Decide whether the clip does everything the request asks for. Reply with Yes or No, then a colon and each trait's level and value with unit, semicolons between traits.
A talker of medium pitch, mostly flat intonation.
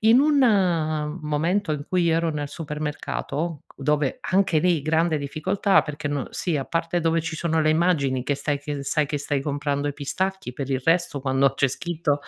No: medium, 155 Hz; average, 3.0 semitones